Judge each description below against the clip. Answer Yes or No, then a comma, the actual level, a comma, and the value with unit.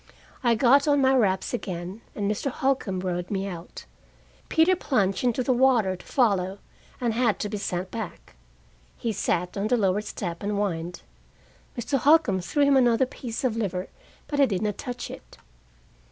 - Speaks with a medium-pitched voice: No, high, 215 Hz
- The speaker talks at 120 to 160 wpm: No, average, 175 wpm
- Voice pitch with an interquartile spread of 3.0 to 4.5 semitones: No, average, 5.2 semitones